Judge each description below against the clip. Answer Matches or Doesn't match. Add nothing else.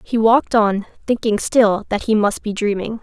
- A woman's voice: Matches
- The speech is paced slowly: Doesn't match